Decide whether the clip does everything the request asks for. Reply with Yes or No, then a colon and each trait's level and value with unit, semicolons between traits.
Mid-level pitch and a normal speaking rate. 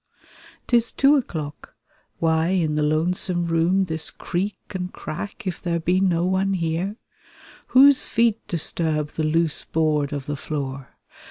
Yes: medium, 170 Hz; average, 145 wpm